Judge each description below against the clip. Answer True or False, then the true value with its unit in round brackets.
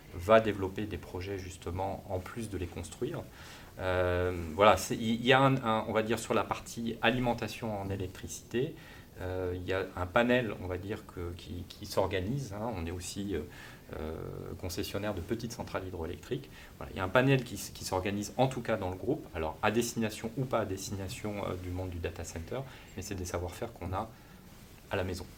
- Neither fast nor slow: True (205 wpm)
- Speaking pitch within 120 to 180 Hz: False (100 Hz)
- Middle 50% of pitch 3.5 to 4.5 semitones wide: True (4.0 semitones)